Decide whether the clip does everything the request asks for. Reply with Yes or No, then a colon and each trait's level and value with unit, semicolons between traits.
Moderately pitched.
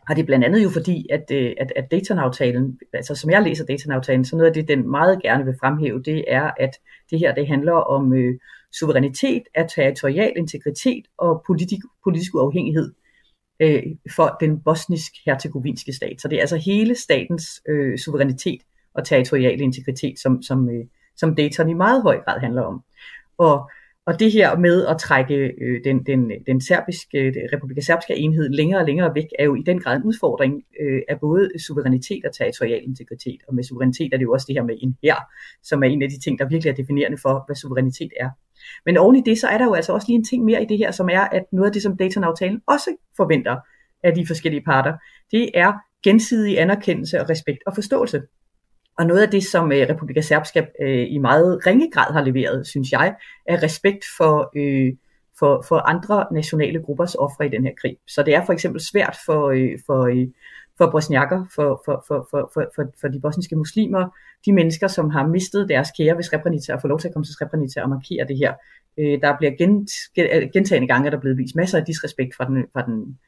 Yes: medium, 155 Hz